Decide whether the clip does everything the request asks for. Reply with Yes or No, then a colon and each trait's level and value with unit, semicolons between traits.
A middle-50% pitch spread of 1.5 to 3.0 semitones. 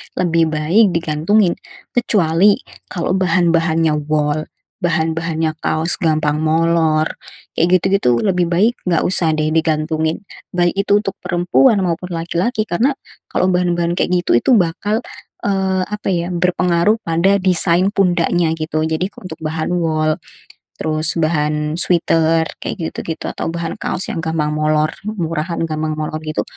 Yes: narrow, 2.5 semitones